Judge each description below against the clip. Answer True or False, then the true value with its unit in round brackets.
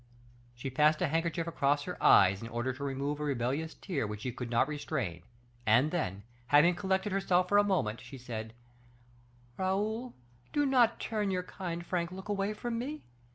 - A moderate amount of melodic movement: False (7.3 semitones)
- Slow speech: False (180 wpm)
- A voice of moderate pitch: True (160 Hz)